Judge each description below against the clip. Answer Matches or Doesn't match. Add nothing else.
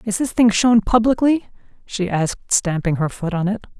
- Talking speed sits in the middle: Matches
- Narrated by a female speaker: Matches